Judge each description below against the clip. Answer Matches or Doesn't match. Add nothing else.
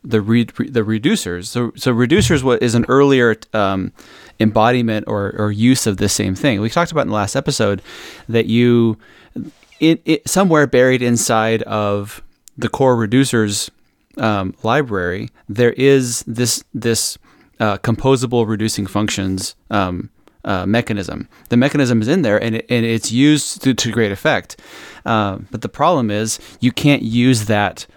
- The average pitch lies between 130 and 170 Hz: Doesn't match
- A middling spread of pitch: Matches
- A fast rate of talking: Doesn't match